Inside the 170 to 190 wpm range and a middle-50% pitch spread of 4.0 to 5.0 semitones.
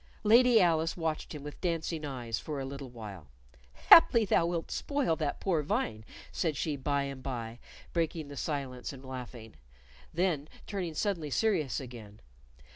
No: average, 155 wpm; average, 4.6 semitones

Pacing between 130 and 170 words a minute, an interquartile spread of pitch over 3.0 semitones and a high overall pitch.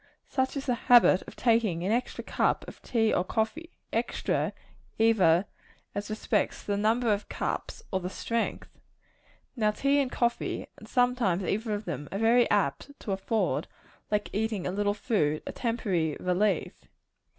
Yes: average, 160 wpm; average, 3.7 semitones; high, 215 Hz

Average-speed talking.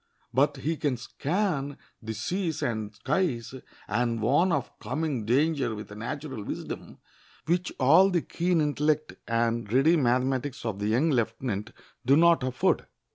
Yes: average, 145 wpm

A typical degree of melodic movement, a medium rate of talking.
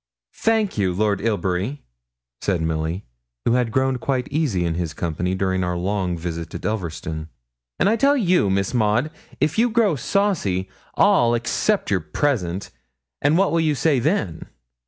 No: wide, 8.9 semitones; average, 160 wpm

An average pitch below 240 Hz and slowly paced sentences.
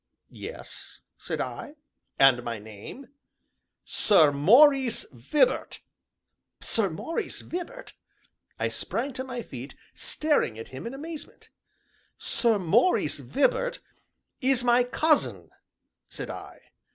No: high, 245 Hz; slow, 105 wpm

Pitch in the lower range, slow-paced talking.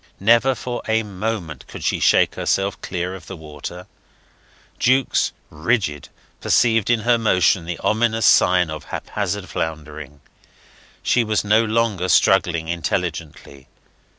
Yes: very low, 95 Hz; slow, 125 wpm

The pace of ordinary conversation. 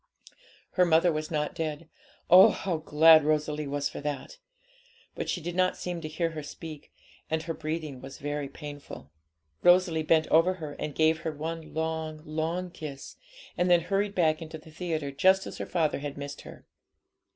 Yes: average, 180 wpm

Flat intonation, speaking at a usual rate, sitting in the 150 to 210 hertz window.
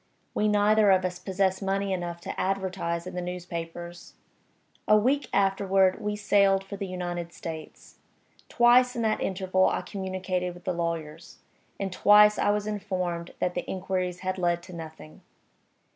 Yes: narrow, 2.3 semitones; average, 160 wpm; medium, 185 Hz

